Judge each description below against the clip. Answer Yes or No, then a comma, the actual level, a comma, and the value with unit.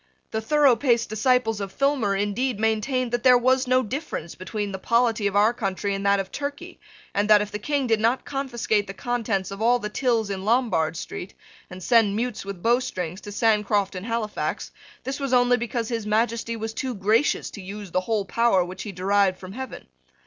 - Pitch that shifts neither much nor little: Yes, average, 3.6 semitones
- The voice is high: Yes, high, 220 Hz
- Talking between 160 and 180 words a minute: No, average, 200 wpm